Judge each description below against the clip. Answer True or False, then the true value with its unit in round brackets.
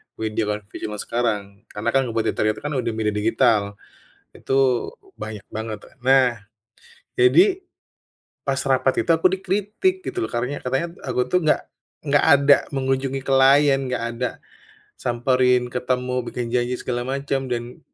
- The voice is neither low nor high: False (125 Hz)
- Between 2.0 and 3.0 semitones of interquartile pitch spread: True (2.6 semitones)